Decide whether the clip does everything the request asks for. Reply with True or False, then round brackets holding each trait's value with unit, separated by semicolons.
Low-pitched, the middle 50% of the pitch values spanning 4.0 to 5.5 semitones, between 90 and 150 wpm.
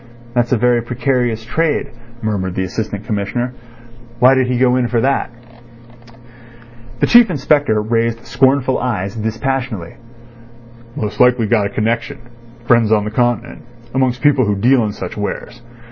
False (120 Hz; 2.8 semitones; 140 wpm)